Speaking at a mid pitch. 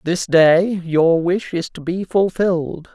Yes: medium, 175 Hz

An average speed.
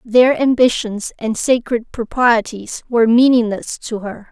No: slow, 125 wpm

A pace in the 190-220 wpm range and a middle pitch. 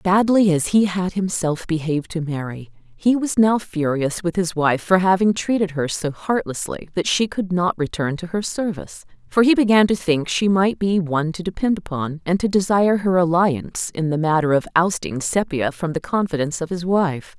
Yes: average, 200 wpm; medium, 175 Hz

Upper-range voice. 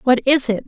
Yes: very high, 255 Hz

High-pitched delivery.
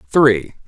No: low, 125 Hz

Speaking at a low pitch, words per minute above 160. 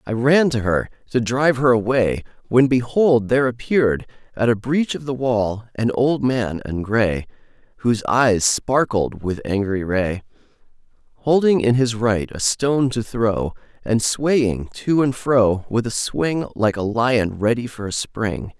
Yes: low, 115 Hz; average, 170 wpm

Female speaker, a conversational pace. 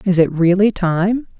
Yes: female; average, 170 wpm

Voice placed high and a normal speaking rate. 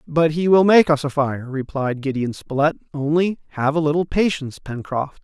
No: medium, 150 Hz; average, 185 wpm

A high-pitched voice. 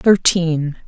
No: medium, 170 Hz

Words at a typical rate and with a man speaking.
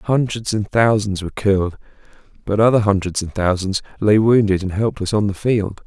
Yes: average, 175 wpm; male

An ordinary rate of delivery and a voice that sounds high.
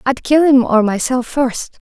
Yes: average, 190 wpm; very high, 255 Hz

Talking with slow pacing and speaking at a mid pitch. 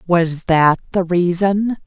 Yes: slow, 130 wpm; medium, 180 Hz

